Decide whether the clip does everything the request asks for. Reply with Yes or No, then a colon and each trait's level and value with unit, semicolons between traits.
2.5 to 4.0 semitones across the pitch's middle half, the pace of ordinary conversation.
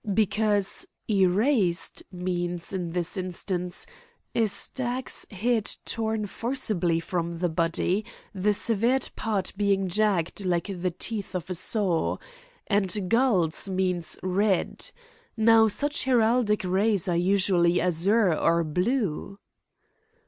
No: average, 3.7 semitones; slow, 110 wpm